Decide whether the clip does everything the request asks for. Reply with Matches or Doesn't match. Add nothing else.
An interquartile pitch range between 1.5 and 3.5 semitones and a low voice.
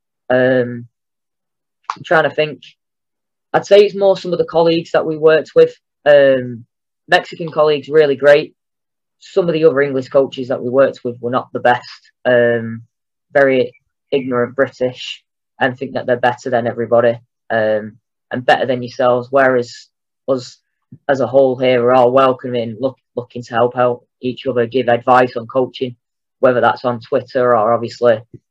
Matches